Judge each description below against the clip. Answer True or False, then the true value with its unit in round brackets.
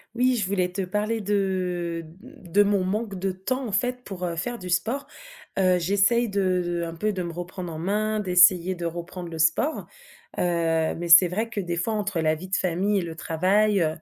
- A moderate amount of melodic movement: True (3.2 semitones)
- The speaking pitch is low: False (185 Hz)